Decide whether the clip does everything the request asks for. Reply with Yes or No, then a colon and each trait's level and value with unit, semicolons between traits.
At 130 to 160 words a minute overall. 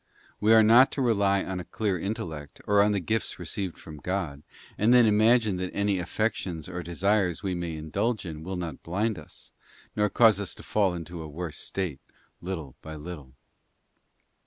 No: average, 180 wpm